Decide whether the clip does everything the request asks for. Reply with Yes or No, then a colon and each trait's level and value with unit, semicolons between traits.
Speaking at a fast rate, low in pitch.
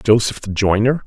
No: average, 170 wpm; low, 110 Hz